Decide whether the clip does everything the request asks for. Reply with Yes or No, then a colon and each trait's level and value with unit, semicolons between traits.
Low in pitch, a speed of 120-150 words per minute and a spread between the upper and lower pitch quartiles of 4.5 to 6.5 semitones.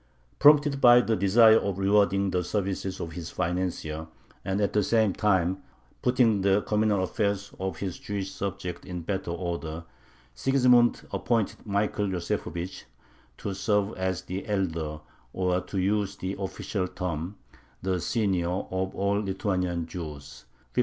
No: very low, 95 Hz; average, 140 wpm; narrow, 2.4 semitones